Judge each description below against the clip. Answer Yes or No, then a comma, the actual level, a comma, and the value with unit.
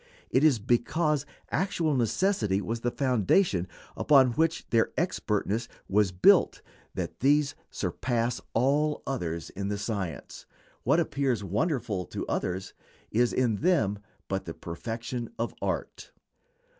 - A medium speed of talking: No, slow, 125 wpm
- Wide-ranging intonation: Yes, wide, 6.2 semitones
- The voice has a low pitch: Yes, low, 120 Hz